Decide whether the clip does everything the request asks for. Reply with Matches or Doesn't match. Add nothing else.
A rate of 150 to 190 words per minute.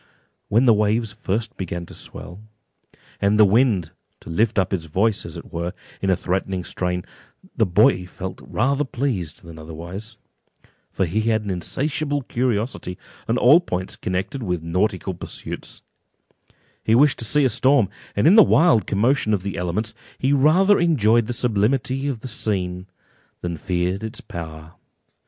Matches